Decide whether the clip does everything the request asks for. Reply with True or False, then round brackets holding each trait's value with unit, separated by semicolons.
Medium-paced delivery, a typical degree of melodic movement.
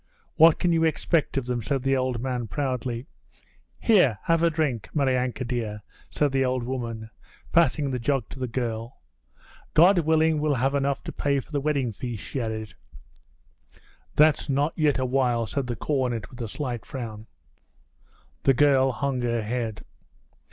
True (165 wpm; 3.4 semitones)